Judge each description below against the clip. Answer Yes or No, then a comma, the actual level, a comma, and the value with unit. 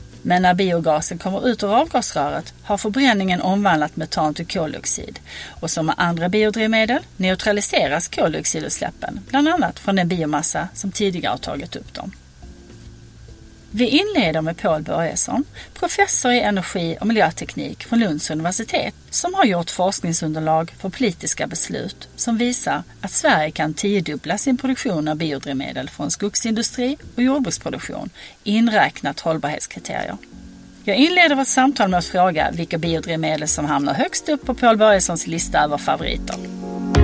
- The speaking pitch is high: Yes, high, 195 Hz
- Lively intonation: Yes, wide, 6.4 semitones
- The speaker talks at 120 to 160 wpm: Yes, average, 140 wpm